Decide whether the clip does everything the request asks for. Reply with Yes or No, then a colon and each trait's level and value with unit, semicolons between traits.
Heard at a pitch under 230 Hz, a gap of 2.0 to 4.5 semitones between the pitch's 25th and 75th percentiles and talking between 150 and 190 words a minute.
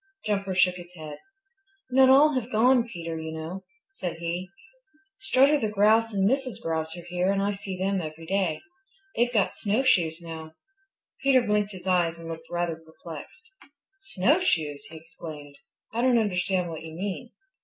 No: medium, 185 Hz; average, 5.3 semitones; average, 165 wpm